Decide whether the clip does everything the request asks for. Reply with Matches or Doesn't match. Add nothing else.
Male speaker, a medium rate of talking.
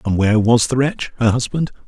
Doesn't match